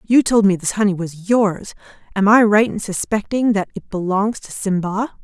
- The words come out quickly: No, average, 195 wpm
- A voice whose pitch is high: Yes, high, 205 Hz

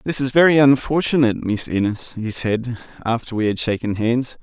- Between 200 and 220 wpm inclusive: No, average, 175 wpm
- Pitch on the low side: Yes, low, 120 Hz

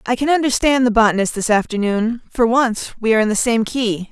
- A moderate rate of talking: No, fast, 220 wpm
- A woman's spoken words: Yes, female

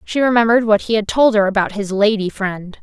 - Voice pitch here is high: Yes, high, 215 Hz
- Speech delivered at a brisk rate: Yes, fast, 235 wpm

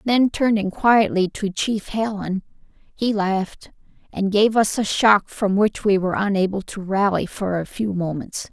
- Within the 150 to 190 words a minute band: Yes, average, 170 wpm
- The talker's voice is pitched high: Yes, high, 200 Hz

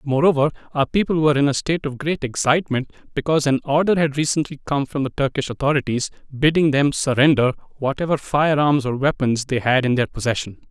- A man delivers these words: Yes, male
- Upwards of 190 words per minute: No, average, 185 wpm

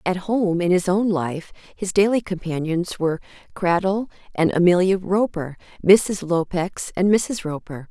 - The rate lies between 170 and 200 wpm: No, average, 145 wpm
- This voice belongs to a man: No, female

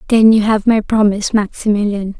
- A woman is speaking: Yes, female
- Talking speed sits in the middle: Yes, average, 165 wpm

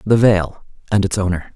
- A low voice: Yes, low, 100 Hz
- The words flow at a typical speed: Yes, average, 195 wpm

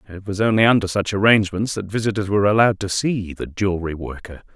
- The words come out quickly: No, average, 195 wpm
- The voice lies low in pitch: Yes, low, 100 Hz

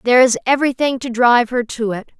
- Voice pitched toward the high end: Yes, high, 245 Hz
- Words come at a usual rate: No, fast, 220 wpm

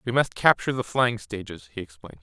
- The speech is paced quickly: Yes, fast, 215 wpm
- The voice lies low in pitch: Yes, low, 115 Hz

